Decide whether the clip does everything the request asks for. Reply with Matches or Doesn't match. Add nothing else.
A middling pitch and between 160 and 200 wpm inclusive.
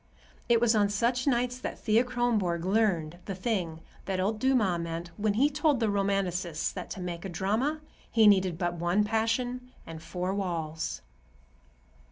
Doesn't match